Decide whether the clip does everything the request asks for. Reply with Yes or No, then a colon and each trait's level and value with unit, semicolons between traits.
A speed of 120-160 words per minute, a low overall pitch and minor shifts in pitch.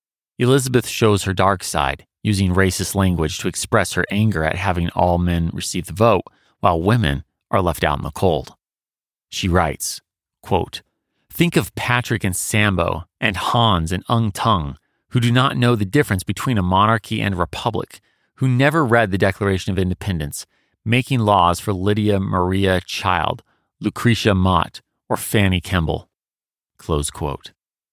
No: average, 150 wpm; low, 100 Hz; average, 4.0 semitones